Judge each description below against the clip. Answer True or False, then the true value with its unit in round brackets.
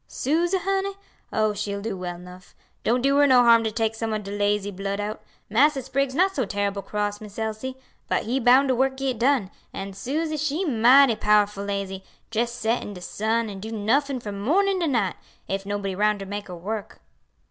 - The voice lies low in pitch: False (220 Hz)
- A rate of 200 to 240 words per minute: True (205 wpm)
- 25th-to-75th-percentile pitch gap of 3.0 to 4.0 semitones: False (4.8 semitones)